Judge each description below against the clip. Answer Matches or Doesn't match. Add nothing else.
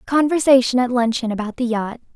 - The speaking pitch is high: Matches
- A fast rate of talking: Doesn't match